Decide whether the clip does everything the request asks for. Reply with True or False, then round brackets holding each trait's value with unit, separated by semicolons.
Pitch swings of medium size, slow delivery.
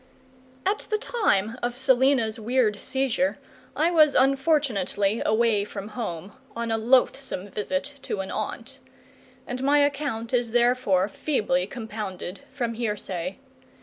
True (4.5 semitones; 125 wpm)